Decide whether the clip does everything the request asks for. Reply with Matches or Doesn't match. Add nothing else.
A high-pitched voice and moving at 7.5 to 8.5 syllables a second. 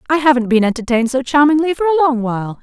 Matches